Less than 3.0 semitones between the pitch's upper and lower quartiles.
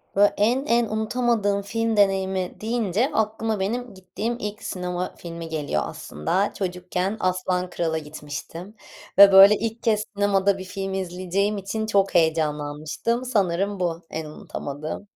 No: average, 3.3 semitones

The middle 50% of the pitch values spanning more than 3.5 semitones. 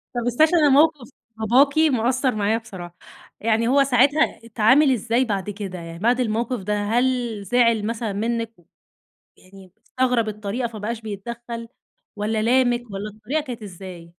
No: average, 3.2 semitones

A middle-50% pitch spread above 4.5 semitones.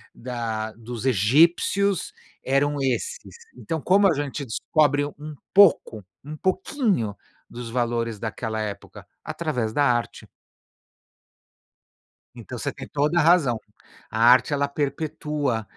Yes: average, 4.9 semitones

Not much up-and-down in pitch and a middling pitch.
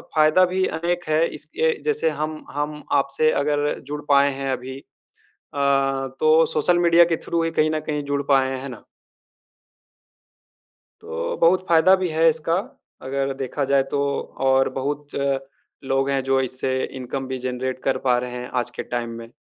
No: average, 3.6 semitones; medium, 145 Hz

